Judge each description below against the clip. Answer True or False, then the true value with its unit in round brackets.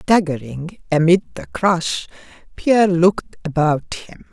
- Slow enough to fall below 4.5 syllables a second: True (4.1 syllables/s)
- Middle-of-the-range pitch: True (175 Hz)